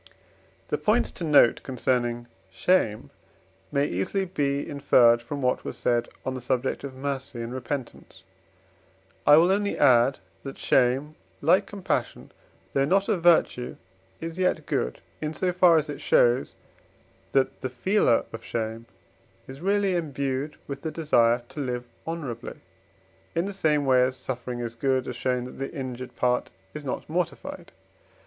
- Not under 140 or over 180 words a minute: Yes, average, 155 wpm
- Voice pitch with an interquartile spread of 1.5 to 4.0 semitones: No, average, 4.4 semitones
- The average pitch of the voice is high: No, low, 135 Hz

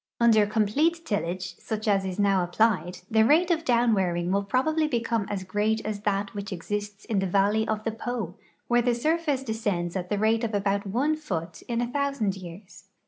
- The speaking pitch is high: Yes, high, 215 Hz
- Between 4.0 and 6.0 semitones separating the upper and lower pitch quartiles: No, average, 3.5 semitones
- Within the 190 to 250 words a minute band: Yes, average, 195 wpm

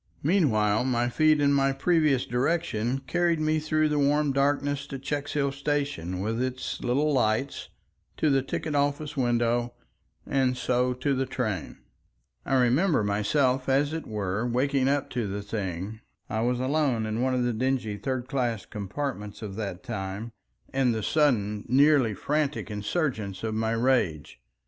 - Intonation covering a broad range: No, average, 4.5 semitones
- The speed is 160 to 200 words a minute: No, average, 150 wpm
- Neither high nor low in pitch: No, low, 130 Hz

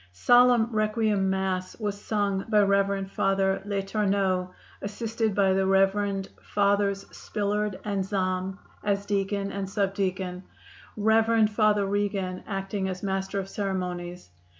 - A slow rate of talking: Yes, slow, 120 wpm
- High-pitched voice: Yes, high, 200 Hz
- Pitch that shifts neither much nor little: No, narrow, 1.3 semitones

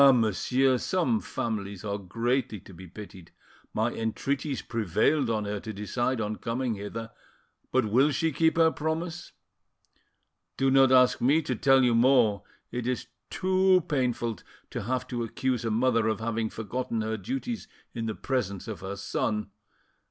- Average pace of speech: Yes, average, 160 wpm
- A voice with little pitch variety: No, average, 3.8 semitones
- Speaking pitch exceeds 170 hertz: No, low, 120 Hz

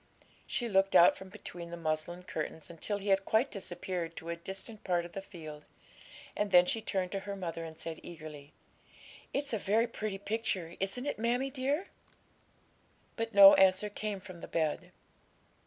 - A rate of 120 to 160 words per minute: No, average, 175 wpm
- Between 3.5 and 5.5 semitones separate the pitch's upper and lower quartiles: Yes, average, 3.9 semitones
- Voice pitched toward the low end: No, high, 190 Hz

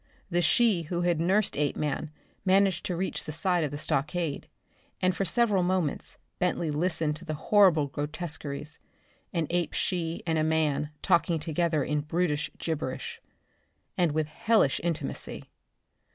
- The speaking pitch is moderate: Yes, medium, 165 Hz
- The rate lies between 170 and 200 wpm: No, average, 145 wpm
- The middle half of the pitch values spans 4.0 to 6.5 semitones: No, average, 3.1 semitones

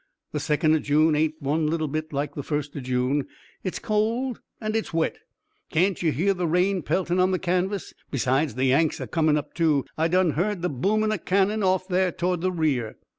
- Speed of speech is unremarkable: No, fast, 210 wpm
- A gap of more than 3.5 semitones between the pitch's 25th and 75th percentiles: Yes, average, 4.0 semitones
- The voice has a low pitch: No, medium, 165 Hz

